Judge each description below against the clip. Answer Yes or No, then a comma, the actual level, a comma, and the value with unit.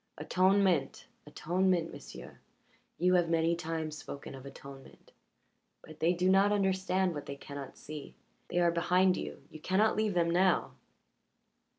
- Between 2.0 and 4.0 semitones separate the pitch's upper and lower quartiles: Yes, average, 3.4 semitones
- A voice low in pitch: No, medium, 170 Hz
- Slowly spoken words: No, average, 145 wpm